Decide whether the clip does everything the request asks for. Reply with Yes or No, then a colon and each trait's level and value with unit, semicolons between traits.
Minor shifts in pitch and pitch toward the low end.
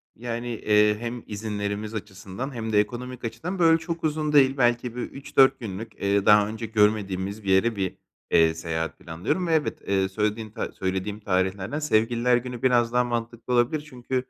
No: average, 3.5 semitones; low, 115 Hz